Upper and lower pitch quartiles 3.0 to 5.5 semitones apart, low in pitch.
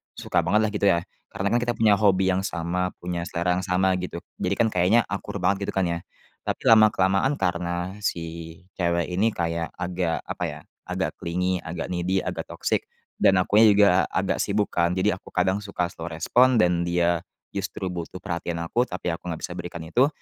No: narrow, 2.4 semitones; very low, 90 Hz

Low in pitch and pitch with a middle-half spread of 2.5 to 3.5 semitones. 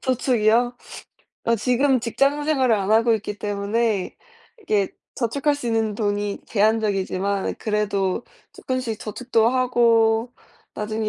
No: high, 225 Hz; average, 3.0 semitones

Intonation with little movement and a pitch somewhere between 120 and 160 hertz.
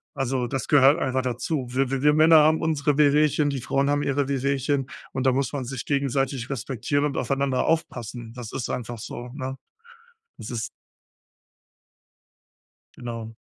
Yes: narrow, 2.3 semitones; low, 135 Hz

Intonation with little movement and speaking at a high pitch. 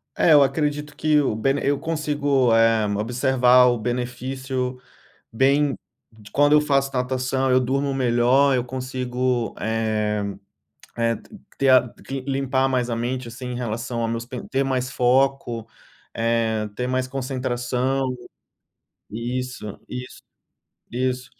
No: narrow, 2.1 semitones; low, 125 Hz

